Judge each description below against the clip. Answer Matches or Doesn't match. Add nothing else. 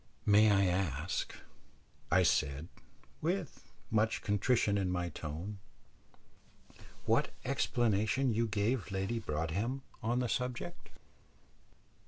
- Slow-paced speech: Matches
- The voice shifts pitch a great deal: Doesn't match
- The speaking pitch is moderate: Doesn't match